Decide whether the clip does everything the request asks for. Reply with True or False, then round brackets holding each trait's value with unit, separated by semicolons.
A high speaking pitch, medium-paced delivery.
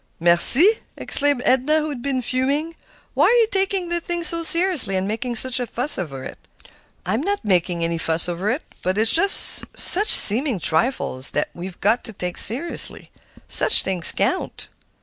True (245 Hz; 175 wpm)